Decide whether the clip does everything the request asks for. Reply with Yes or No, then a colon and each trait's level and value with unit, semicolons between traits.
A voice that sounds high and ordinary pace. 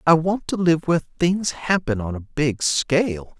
No: medium, 155 Hz; average, 195 wpm